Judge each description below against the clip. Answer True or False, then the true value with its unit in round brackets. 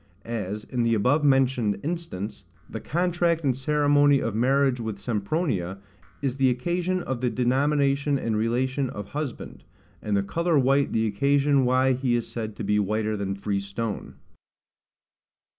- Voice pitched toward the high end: False (130 Hz)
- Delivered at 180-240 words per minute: False (155 wpm)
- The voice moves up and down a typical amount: True (4.9 semitones)